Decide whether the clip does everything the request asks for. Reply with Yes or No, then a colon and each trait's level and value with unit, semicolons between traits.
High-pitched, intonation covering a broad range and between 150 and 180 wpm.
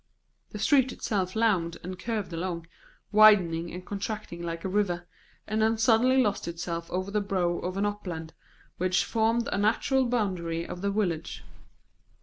No: high, 195 Hz; average, 3.9 semitones; average, 155 wpm